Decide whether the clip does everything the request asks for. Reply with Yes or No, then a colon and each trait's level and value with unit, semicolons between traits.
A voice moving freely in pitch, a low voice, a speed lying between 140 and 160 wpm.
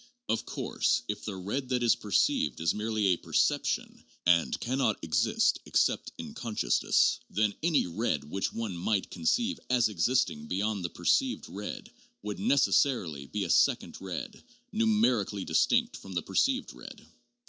Yes: wide, 5.9 semitones; low, 105 Hz; average, 150 wpm